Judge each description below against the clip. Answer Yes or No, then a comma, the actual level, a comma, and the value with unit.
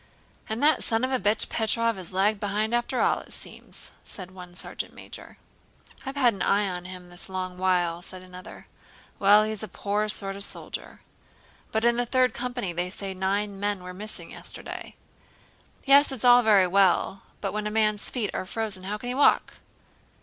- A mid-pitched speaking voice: No, high, 205 Hz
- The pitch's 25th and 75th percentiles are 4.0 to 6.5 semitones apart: No, average, 3.4 semitones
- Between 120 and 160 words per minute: No, average, 195 wpm